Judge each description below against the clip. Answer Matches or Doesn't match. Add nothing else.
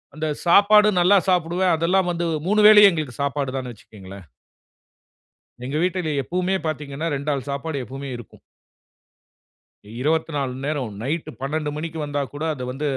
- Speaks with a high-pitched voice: Doesn't match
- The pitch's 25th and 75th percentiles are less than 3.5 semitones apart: Doesn't match